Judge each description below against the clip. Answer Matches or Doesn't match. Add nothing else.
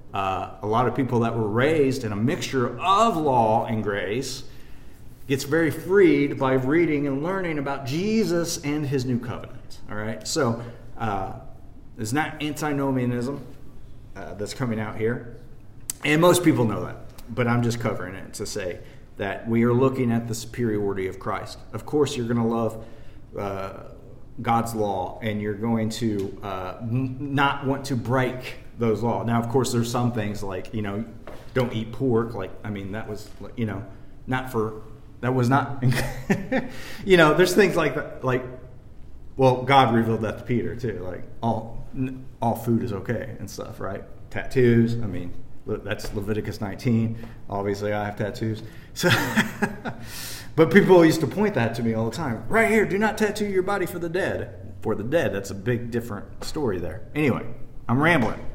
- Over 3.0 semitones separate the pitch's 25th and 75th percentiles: Matches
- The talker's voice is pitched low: Matches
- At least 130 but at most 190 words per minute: Matches